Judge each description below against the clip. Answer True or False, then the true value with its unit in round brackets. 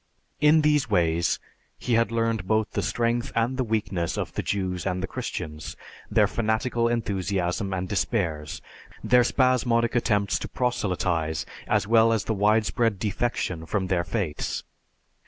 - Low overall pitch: True (105 Hz)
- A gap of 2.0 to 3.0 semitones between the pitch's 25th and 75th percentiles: False (4.2 semitones)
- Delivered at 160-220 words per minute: False (140 wpm)